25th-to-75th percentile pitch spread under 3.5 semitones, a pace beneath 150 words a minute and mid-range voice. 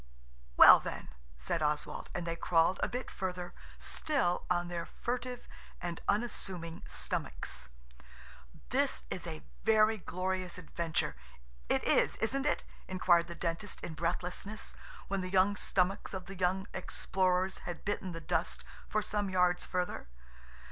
Yes: average, 2.7 semitones; average, 140 wpm; medium, 180 Hz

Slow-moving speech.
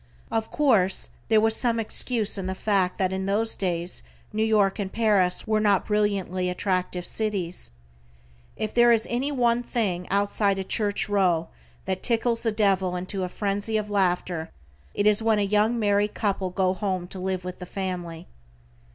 No: average, 175 wpm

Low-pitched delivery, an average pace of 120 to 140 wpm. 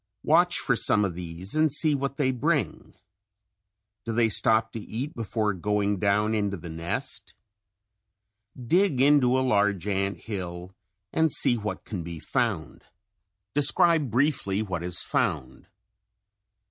Yes: low, 110 Hz; slow, 135 wpm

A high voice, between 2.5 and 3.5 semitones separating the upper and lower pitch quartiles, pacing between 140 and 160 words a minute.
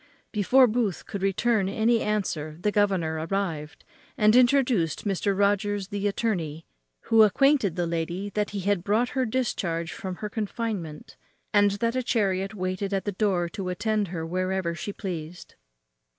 Yes: high, 200 Hz; average, 3.2 semitones; average, 155 wpm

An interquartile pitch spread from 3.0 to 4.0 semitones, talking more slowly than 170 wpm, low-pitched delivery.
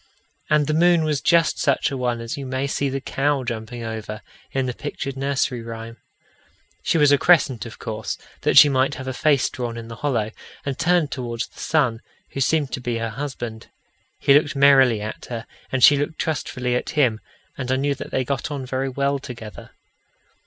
No: average, 3.3 semitones; average, 200 wpm; low, 130 Hz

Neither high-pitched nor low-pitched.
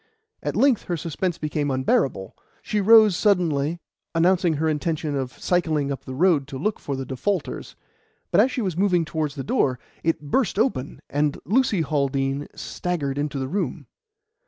Yes: medium, 155 Hz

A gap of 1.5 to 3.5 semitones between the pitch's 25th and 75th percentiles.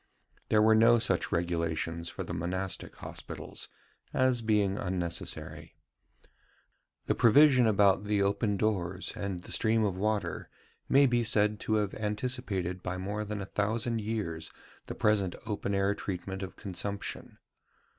Yes: average, 2.8 semitones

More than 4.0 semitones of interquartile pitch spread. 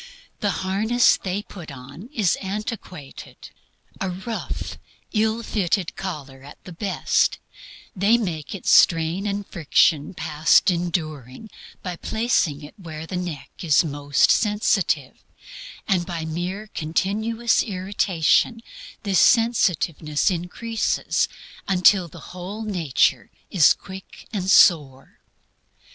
Yes: average, 4.5 semitones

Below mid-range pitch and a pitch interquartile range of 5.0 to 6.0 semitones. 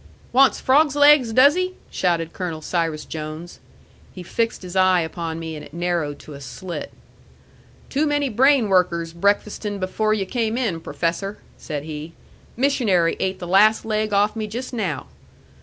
No: high, 190 Hz; wide, 5.5 semitones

